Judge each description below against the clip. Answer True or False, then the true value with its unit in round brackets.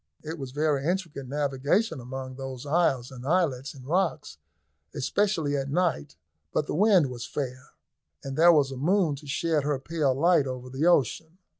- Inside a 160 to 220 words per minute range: True (170 wpm)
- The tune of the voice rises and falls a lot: False (4.0 semitones)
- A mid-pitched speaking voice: True (145 Hz)